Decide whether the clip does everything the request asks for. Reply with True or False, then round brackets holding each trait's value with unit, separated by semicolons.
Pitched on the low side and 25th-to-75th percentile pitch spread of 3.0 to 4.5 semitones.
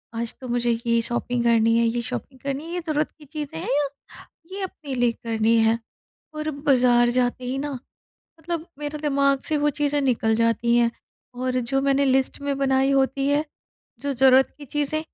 False (265 Hz; 3.4 semitones)